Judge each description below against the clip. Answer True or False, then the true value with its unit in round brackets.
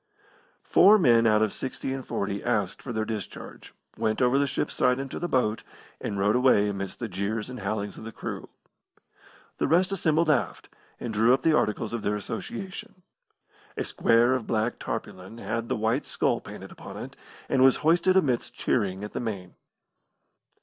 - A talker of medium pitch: False (115 Hz)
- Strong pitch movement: False (4.1 semitones)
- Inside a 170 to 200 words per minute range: True (180 wpm)